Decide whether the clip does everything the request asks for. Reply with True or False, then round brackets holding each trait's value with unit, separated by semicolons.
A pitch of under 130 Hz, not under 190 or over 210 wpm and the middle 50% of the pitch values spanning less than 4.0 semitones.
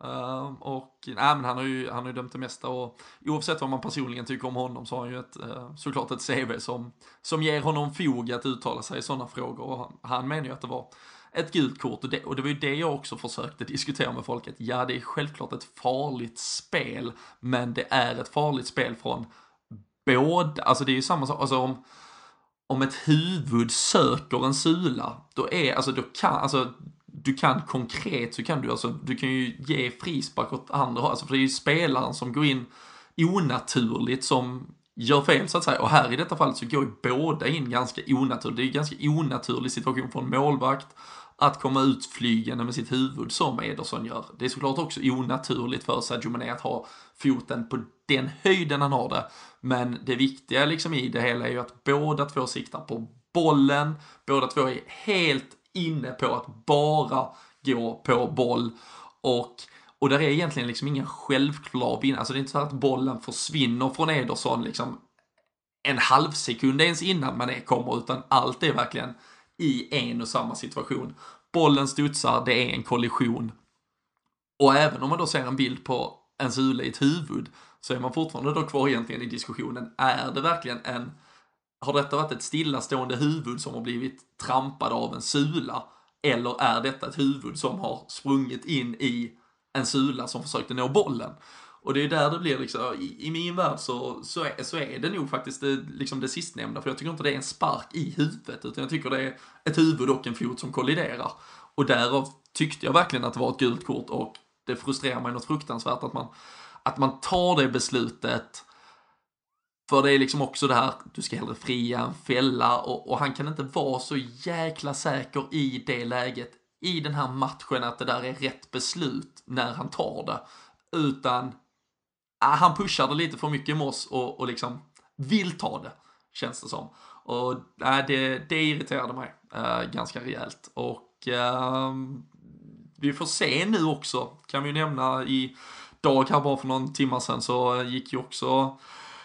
False (135 Hz; 195 wpm; 2.5 semitones)